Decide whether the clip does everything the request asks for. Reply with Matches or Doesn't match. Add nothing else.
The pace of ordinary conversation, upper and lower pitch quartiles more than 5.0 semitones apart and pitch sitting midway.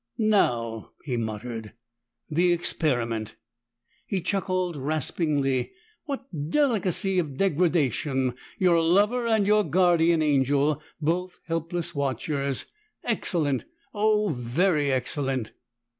Doesn't match